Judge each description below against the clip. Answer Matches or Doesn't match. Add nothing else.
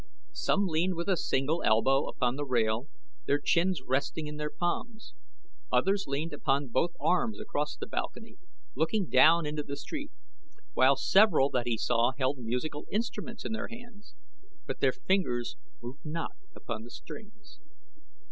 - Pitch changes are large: Matches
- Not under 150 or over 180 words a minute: Matches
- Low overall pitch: Doesn't match